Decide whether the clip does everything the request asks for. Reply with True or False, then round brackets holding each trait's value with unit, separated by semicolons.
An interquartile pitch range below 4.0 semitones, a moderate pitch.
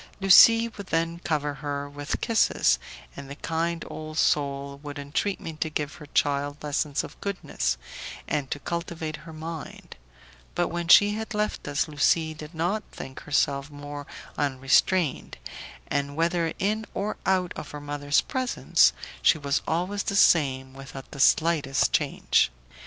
True (3.2 semitones; 155 Hz)